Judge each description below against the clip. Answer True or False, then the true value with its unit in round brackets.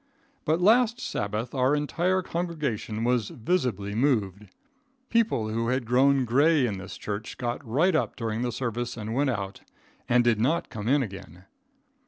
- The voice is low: True (125 Hz)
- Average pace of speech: True (160 wpm)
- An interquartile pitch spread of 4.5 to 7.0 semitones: True (5.3 semitones)